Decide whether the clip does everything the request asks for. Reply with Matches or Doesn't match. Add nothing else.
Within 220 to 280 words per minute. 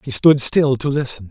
Matches